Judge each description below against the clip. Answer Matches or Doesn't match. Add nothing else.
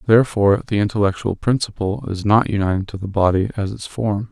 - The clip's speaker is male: Matches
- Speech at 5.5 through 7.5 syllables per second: Matches